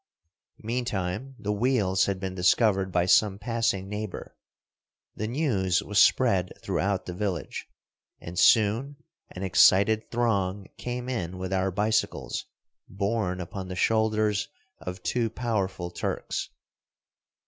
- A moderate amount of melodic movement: Yes, average, 3.3 semitones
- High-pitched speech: No, low, 100 Hz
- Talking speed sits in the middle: No, slow, 120 wpm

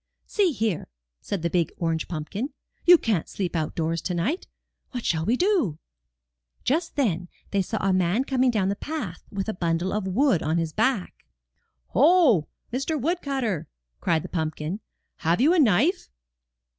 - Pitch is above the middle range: Yes, high, 200 Hz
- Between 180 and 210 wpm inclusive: No, average, 165 wpm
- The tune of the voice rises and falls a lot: Yes, wide, 8.0 semitones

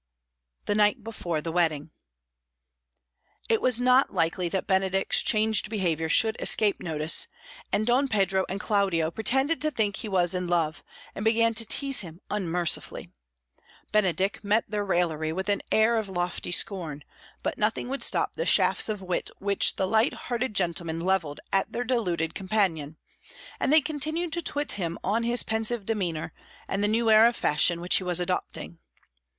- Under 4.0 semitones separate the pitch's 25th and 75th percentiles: No, average, 4.4 semitones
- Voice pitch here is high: Yes, high, 200 Hz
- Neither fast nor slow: Yes, average, 165 wpm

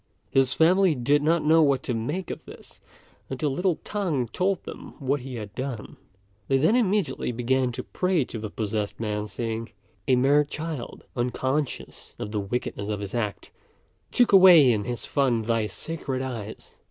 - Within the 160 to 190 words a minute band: Yes, average, 170 wpm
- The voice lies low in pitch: Yes, low, 130 Hz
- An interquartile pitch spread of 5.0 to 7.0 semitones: Yes, wide, 5.5 semitones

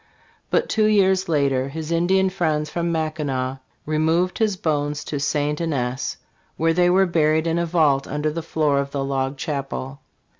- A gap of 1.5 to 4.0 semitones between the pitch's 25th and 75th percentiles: Yes, average, 3.4 semitones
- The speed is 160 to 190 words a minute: Yes, average, 165 wpm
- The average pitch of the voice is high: No, medium, 155 Hz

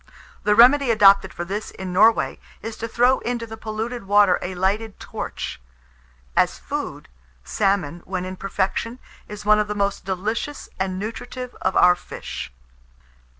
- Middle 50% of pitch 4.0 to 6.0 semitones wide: No, average, 3.1 semitones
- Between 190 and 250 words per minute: No, average, 150 wpm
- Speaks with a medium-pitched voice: No, high, 205 Hz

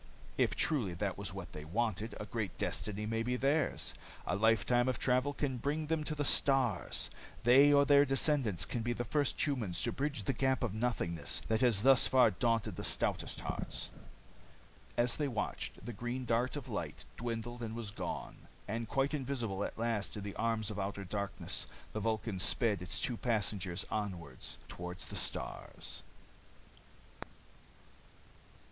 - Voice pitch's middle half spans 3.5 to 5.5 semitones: Yes, average, 4.2 semitones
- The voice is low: Yes, low, 115 Hz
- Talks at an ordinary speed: Yes, average, 165 wpm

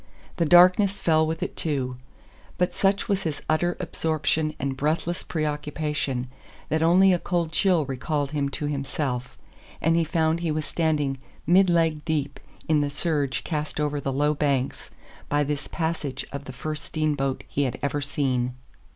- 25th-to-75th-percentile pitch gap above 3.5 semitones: No, narrow, 2.6 semitones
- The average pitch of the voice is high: No, medium, 150 Hz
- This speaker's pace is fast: No, average, 165 wpm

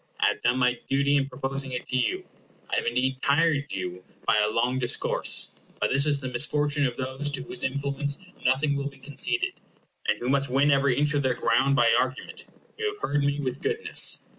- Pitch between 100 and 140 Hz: Yes, low, 135 Hz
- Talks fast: Yes, fast, 210 wpm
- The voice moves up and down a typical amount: No, narrow, 2.1 semitones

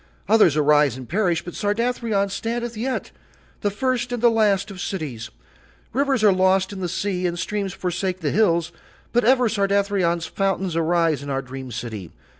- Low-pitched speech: No, high, 190 Hz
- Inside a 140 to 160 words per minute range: No, average, 170 wpm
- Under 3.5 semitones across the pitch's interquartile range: No, average, 4.5 semitones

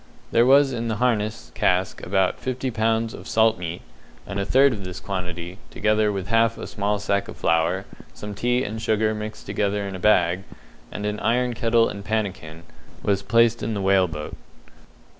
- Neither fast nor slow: Yes, average, 185 wpm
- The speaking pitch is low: Yes, low, 105 Hz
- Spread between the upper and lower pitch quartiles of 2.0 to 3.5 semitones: Yes, average, 3.0 semitones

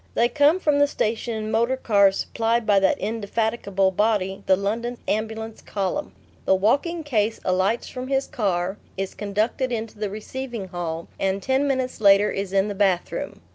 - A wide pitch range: No, average, 3.5 semitones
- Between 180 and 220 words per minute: No, average, 170 wpm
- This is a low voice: No, high, 215 Hz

